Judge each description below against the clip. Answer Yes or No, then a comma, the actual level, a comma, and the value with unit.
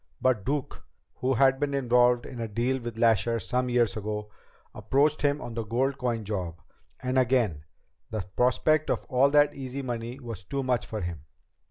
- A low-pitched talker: Yes, low, 125 Hz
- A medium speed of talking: Yes, average, 180 wpm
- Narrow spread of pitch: No, average, 3.2 semitones